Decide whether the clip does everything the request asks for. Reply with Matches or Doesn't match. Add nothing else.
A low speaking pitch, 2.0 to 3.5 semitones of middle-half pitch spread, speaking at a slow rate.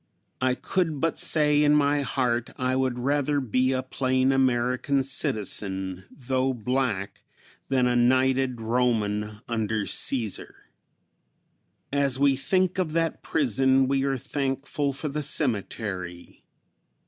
Matches